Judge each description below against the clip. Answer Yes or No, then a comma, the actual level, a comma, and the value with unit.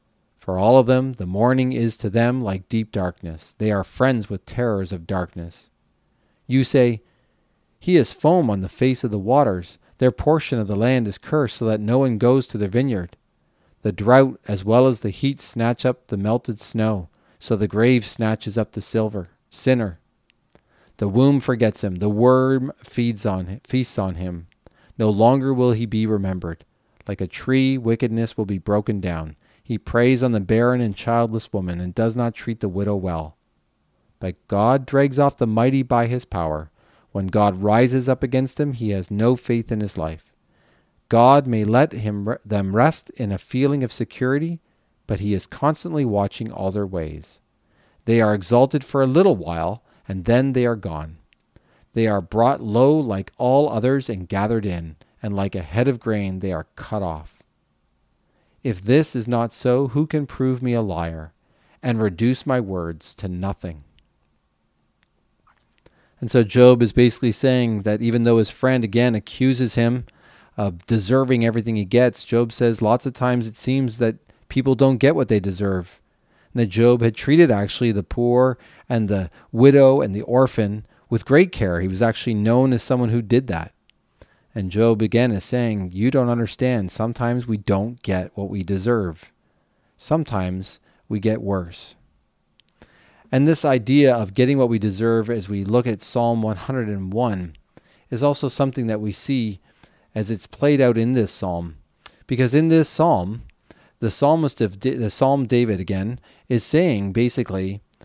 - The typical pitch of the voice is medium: No, low, 115 Hz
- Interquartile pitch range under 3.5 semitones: No, average, 4.0 semitones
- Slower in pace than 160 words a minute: No, average, 175 wpm